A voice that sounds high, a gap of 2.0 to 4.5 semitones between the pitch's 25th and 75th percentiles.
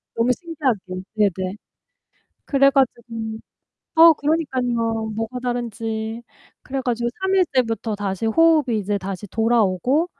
Yes: high, 235 Hz; average, 3.9 semitones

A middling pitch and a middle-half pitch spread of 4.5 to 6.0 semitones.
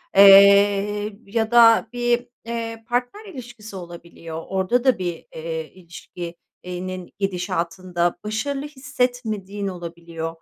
No: high, 200 Hz; average, 5.0 semitones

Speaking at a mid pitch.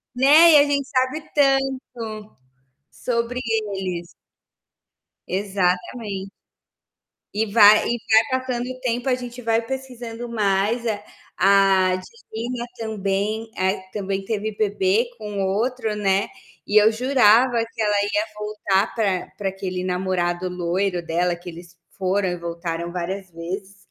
No: high, 210 Hz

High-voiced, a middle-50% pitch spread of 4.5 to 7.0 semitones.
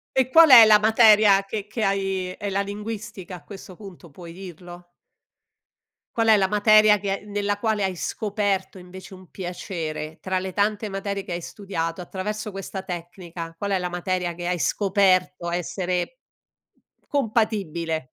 No: high, 195 Hz; average, 2.8 semitones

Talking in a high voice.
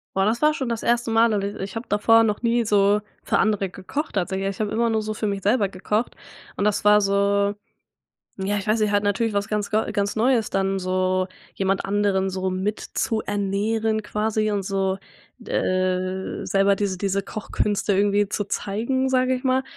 Yes: high, 205 Hz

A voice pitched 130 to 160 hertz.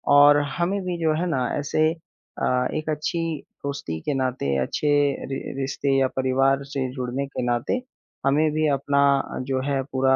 Yes: medium, 140 Hz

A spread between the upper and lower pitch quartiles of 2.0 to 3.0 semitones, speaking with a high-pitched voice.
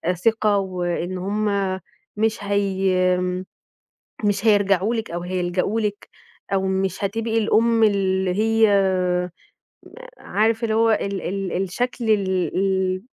Yes: average, 2.7 semitones; high, 200 Hz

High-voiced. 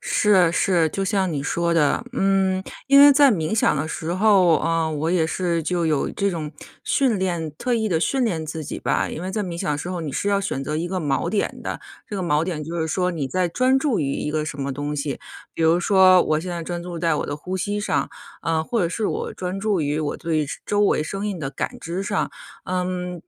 No: medium, 175 Hz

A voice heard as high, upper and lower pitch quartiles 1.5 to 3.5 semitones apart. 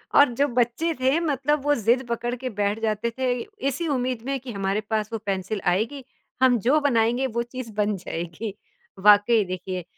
No: high, 235 Hz; average, 4.0 semitones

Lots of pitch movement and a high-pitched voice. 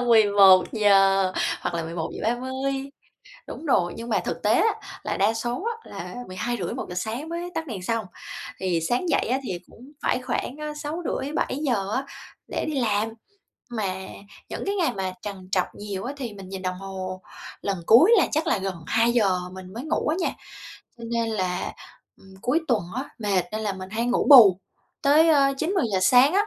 Yes: wide, 6.2 semitones; high, 225 Hz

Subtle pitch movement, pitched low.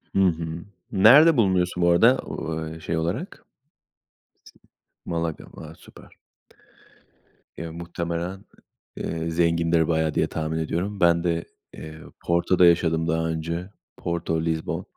Yes: narrow, 1.3 semitones; very low, 85 Hz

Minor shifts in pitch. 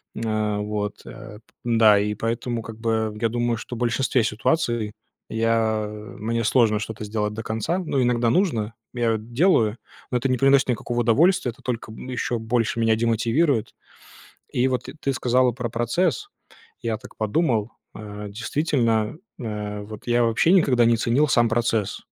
Yes: narrow, 2.3 semitones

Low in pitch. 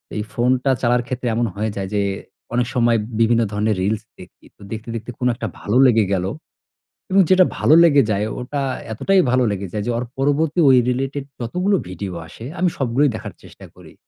Yes: low, 120 Hz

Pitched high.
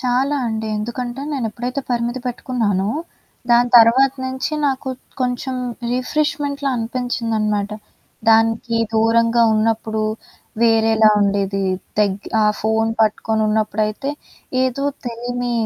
Yes: high, 230 Hz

